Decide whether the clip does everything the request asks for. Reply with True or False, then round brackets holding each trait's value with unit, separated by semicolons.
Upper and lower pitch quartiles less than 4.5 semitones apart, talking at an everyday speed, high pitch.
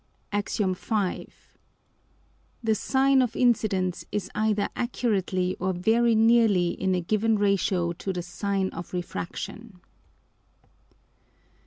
False (3.4 semitones; 115 wpm; 200 Hz)